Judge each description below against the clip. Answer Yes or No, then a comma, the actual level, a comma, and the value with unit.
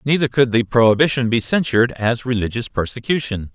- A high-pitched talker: No, low, 120 Hz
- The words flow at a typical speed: Yes, average, 150 wpm